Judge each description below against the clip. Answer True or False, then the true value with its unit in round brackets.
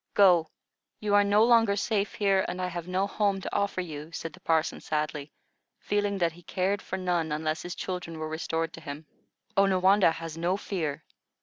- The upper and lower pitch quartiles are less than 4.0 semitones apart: True (3.6 semitones)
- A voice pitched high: False (180 Hz)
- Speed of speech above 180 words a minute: True (190 wpm)